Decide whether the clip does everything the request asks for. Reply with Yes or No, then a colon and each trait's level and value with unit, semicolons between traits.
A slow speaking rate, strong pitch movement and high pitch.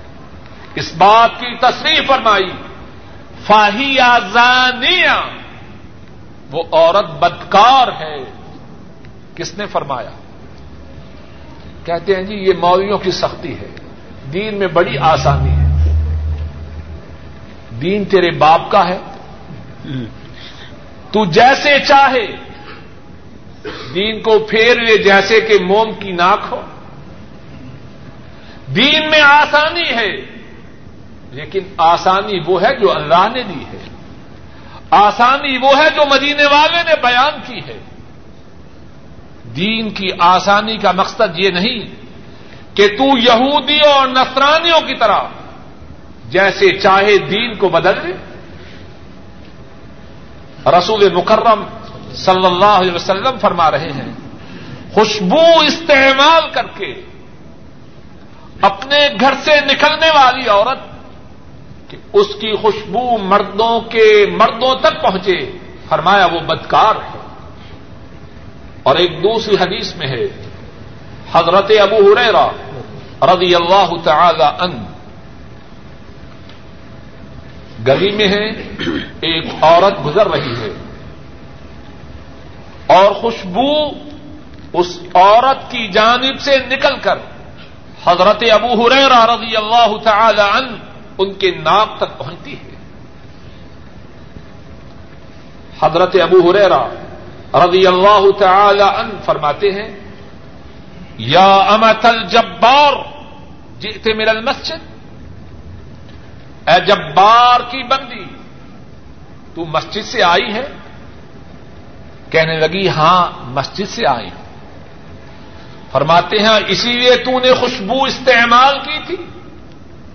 Yes: slow, 100 wpm; wide, 6.1 semitones; high, 205 Hz